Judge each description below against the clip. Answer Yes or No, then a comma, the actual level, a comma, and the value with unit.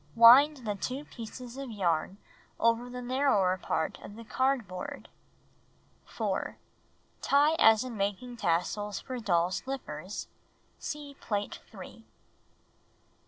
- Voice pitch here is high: Yes, high, 230 Hz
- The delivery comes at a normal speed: No, slow, 120 wpm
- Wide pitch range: No, average, 4.7 semitones